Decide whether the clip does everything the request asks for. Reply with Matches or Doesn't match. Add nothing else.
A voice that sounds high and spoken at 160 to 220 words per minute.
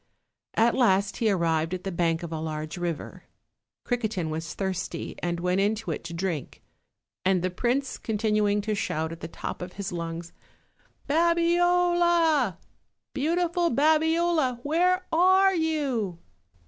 Doesn't match